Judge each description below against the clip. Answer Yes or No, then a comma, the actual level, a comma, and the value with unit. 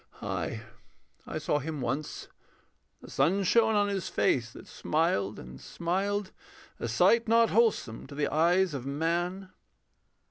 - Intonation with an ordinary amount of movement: No, wide, 5.8 semitones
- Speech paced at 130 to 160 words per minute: Yes, average, 140 wpm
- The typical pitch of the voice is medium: Yes, medium, 170 Hz